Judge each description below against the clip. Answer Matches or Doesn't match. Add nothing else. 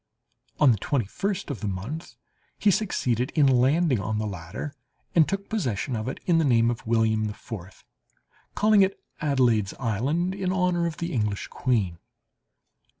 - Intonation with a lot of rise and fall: Matches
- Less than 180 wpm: Matches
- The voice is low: Matches